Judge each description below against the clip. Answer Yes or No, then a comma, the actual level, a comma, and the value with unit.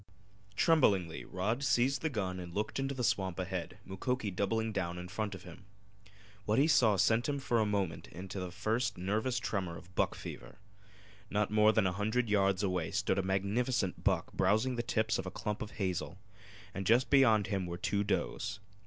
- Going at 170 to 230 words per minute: Yes, average, 190 wpm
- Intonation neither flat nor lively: Yes, average, 3.4 semitones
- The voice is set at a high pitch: No, low, 105 Hz